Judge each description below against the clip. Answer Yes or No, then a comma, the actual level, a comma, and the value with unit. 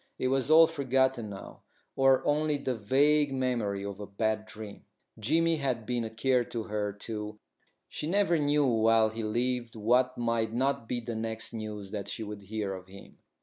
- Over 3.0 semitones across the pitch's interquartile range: Yes, average, 3.9 semitones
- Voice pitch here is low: Yes, low, 115 Hz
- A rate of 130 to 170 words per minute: No, average, 185 wpm